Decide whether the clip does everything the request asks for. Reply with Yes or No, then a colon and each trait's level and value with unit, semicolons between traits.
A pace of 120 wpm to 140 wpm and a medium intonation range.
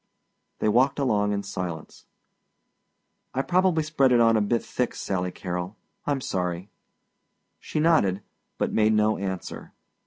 No: slow, 135 wpm; wide, 6.1 semitones